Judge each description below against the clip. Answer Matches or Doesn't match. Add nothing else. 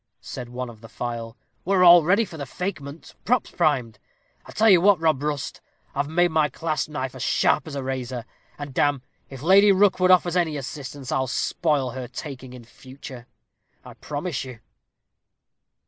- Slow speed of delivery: Doesn't match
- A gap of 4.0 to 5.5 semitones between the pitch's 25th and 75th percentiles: Matches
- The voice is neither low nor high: Matches